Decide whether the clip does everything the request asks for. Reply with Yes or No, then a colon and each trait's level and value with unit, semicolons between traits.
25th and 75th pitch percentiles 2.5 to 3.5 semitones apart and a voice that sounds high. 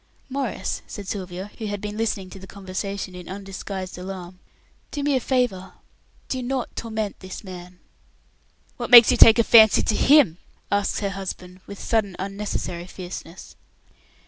Yes: average, 3.2 semitones; high, 200 Hz